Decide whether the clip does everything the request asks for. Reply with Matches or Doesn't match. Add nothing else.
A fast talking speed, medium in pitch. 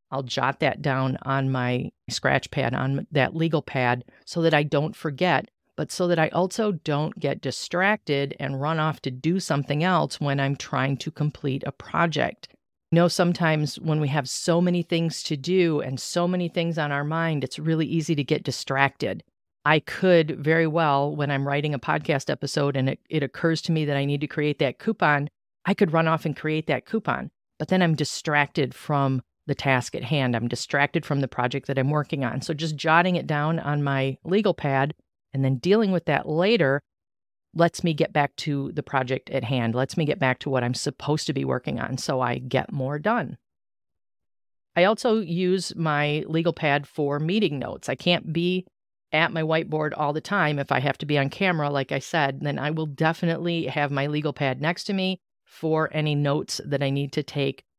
Matches